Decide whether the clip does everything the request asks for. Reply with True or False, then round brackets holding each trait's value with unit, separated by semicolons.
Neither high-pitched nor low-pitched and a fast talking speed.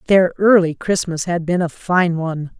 False (175 Hz; 185 wpm)